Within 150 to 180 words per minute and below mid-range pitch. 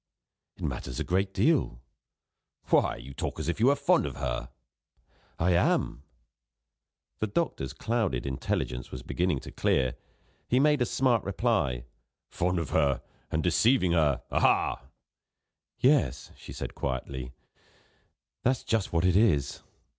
No: average, 140 wpm; very low, 85 Hz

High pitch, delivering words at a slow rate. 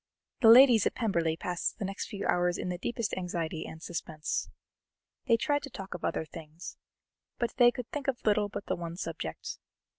No: high, 195 Hz; average, 190 wpm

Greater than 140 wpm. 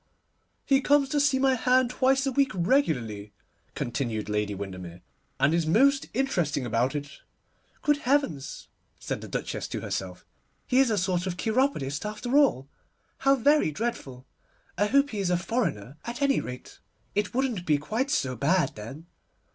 Yes: average, 165 wpm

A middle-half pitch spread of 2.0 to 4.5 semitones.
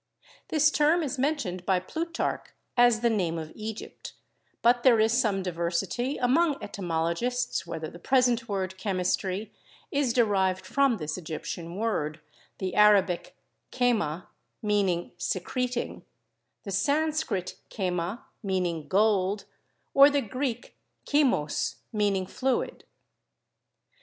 No: wide, 5.5 semitones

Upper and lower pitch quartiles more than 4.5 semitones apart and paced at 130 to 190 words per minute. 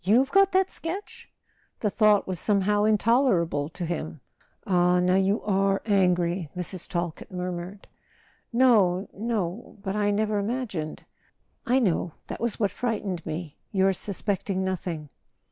No: average, 3.3 semitones; average, 145 wpm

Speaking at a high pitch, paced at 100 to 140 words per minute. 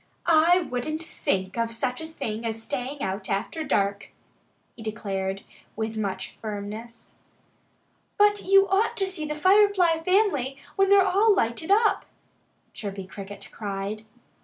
Yes: very high, 250 Hz; slow, 135 wpm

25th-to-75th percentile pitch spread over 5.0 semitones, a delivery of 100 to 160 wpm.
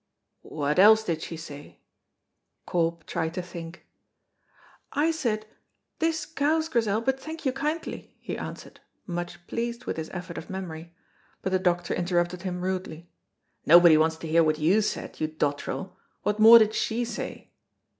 Yes: wide, 5.5 semitones; average, 155 wpm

